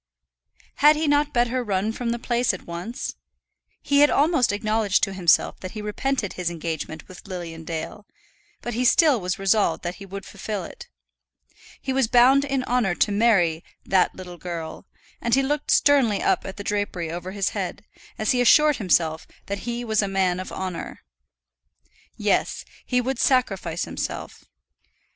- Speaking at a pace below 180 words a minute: Yes, average, 170 wpm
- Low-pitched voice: No, high, 205 Hz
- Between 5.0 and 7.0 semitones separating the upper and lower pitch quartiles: Yes, wide, 5.4 semitones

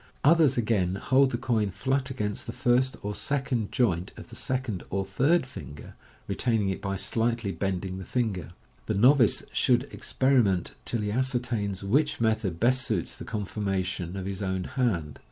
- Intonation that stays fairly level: No, average, 4.9 semitones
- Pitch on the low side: Yes, low, 110 Hz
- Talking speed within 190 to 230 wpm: No, average, 165 wpm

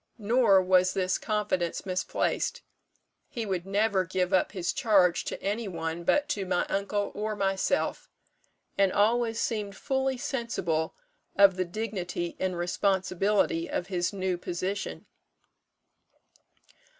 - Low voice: No, high, 195 Hz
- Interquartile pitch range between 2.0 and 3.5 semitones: Yes, average, 2.9 semitones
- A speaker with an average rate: No, slow, 125 wpm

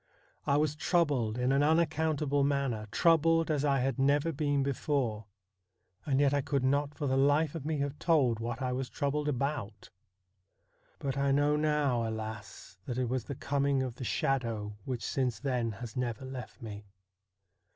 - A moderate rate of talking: Yes, average, 170 wpm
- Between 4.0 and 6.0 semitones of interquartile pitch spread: No, average, 3.0 semitones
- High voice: No, low, 135 Hz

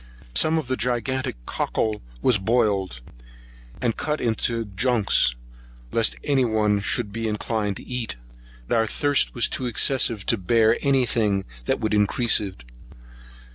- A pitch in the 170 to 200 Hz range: No, low, 115 Hz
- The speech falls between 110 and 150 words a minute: Yes, average, 145 wpm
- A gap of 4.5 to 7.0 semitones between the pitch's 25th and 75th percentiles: No, average, 3.2 semitones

